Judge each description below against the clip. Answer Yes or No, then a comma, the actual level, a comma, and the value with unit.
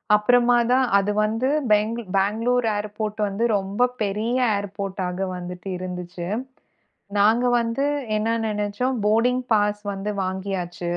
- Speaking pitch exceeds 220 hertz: No, high, 210 Hz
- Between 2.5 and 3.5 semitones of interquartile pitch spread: Yes, average, 2.9 semitones